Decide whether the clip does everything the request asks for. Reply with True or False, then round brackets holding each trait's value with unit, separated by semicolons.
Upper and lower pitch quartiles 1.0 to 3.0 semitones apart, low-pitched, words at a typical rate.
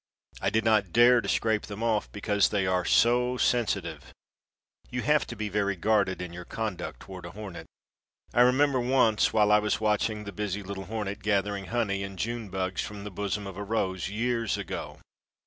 True (2.6 semitones; 105 Hz; 190 wpm)